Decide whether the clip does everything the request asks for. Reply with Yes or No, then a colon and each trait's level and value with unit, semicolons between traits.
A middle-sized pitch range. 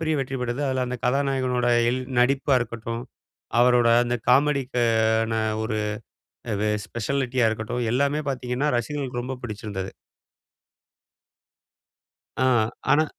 No: narrow, 2.2 semitones